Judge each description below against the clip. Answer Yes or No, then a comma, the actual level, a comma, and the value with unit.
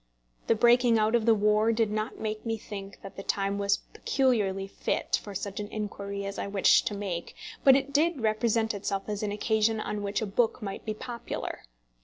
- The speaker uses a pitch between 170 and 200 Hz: No, high, 215 Hz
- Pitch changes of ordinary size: No, narrow, 2.2 semitones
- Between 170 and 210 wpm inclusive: Yes, average, 200 wpm